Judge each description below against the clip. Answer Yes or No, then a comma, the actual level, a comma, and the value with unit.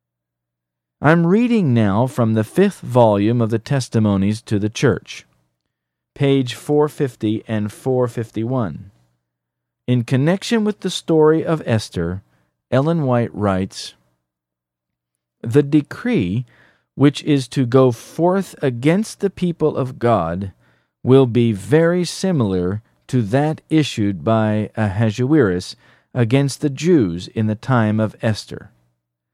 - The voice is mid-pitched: No, low, 120 Hz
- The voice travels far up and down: Yes, wide, 7.0 semitones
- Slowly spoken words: Yes, slow, 115 wpm